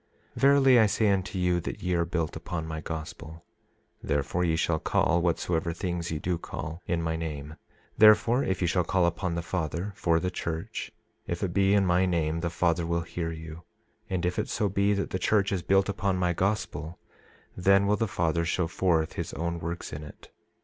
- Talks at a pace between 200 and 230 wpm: Yes, fast, 205 wpm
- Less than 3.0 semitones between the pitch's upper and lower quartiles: Yes, narrow, 2.6 semitones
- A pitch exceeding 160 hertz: No, very low, 85 Hz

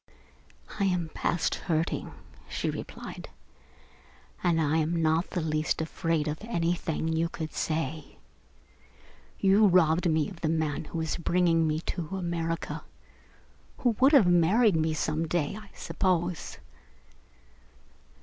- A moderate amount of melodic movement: No, narrow, 2.1 semitones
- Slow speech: Yes, slow, 130 wpm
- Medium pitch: Yes, medium, 165 Hz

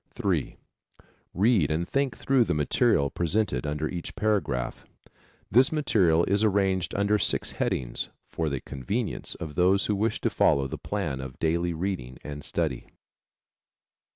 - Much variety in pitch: Yes, wide, 5.9 semitones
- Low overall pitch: Yes, very low, 90 Hz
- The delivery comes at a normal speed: Yes, average, 145 wpm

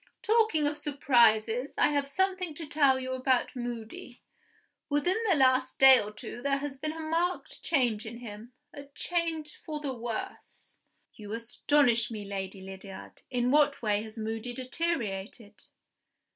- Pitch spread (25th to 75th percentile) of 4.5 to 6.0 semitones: Yes, average, 4.8 semitones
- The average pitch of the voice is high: Yes, very high, 255 Hz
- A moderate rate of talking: Yes, average, 150 wpm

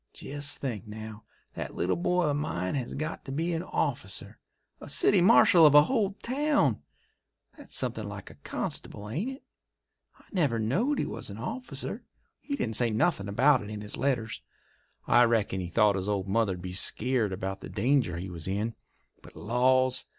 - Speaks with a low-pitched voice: Yes, low, 120 Hz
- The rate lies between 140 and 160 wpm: No, average, 180 wpm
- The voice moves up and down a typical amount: No, wide, 6.8 semitones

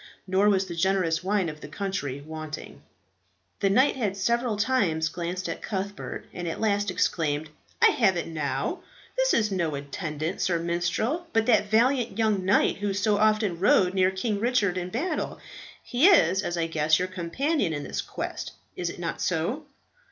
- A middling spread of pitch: Yes, average, 4.4 semitones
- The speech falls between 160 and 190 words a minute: Yes, average, 175 wpm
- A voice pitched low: No, high, 190 Hz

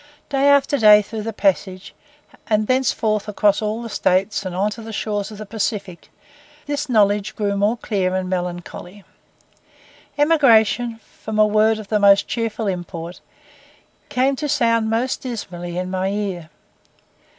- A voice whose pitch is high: Yes, high, 210 Hz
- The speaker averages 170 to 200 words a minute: No, average, 150 wpm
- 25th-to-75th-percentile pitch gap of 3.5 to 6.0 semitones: No, average, 2.8 semitones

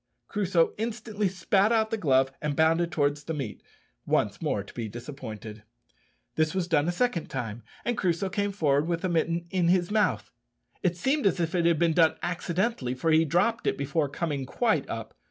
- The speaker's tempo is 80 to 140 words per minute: No, average, 190 wpm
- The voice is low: No, medium, 170 Hz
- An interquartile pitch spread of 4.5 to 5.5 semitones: Yes, average, 4.8 semitones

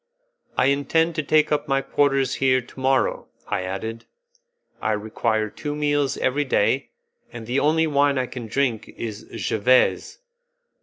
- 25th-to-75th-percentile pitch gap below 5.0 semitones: Yes, average, 4.1 semitones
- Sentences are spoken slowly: No, average, 150 wpm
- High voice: No, low, 135 Hz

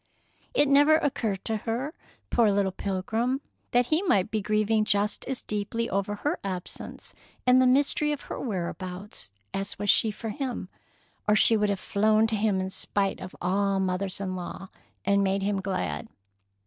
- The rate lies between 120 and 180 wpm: Yes, average, 175 wpm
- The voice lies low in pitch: No, high, 205 Hz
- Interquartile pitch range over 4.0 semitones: No, average, 3.2 semitones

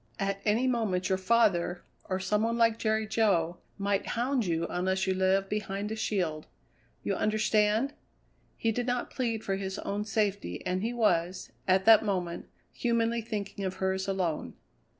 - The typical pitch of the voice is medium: No, high, 200 Hz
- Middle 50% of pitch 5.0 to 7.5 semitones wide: No, average, 2.9 semitones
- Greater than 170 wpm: No, average, 165 wpm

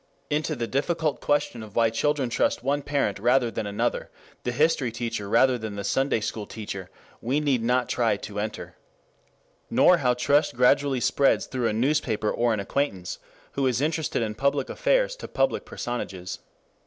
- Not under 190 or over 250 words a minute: No, average, 170 wpm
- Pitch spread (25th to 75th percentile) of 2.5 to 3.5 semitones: No, average, 4.4 semitones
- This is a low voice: Yes, low, 125 Hz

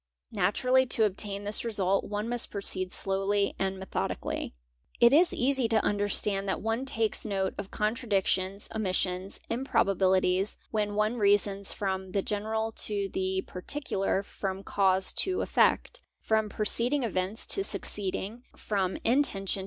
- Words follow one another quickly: No, average, 145 wpm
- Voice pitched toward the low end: No, high, 205 Hz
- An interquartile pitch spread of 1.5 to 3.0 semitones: Yes, narrow, 2.6 semitones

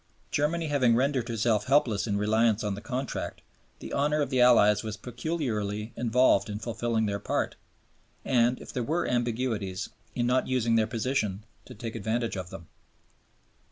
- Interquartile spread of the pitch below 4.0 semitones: Yes, average, 3.2 semitones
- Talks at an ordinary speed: Yes, average, 160 wpm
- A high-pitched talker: No, low, 115 Hz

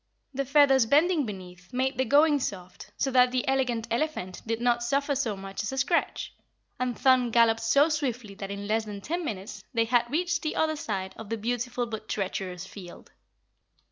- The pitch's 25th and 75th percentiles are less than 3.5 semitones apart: No, average, 4.7 semitones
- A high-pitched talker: Yes, high, 240 Hz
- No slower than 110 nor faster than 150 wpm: No, average, 190 wpm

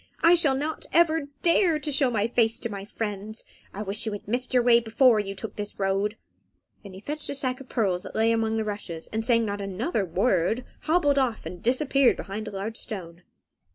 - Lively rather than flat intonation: No, average, 4.6 semitones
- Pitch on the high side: Yes, high, 225 Hz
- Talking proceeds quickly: Yes, fast, 215 wpm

